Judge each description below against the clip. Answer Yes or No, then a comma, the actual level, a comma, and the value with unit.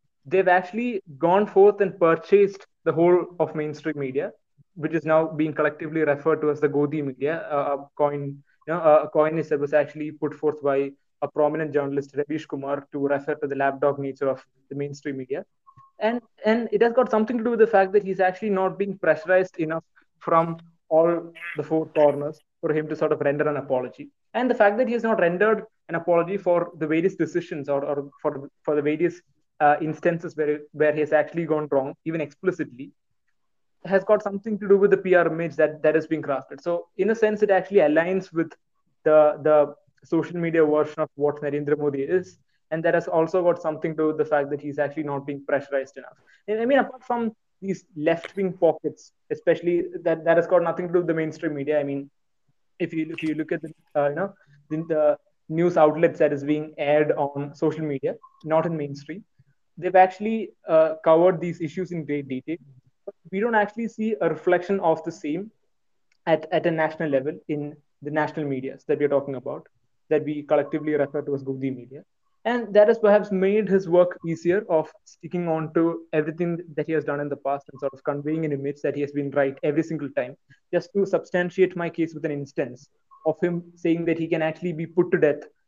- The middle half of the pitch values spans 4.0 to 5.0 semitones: No, average, 3.4 semitones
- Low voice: No, medium, 160 Hz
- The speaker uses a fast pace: Yes, fast, 215 wpm